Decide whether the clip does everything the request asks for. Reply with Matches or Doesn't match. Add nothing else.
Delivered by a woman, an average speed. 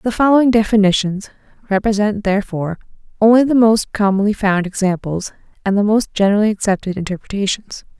Doesn't match